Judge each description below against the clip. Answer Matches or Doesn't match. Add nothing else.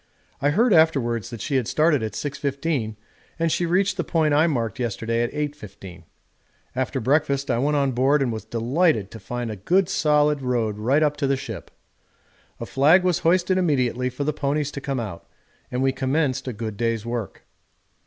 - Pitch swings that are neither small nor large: Matches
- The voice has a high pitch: Doesn't match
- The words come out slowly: Doesn't match